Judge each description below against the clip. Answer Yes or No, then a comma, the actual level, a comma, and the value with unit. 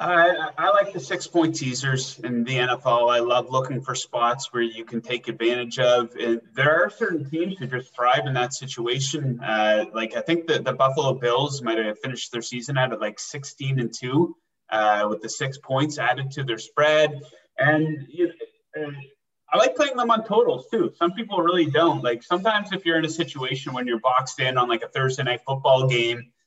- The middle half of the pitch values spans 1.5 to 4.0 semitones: No, average, 4.7 semitones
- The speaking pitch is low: Yes, low, 130 Hz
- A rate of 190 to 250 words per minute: Yes, fast, 205 wpm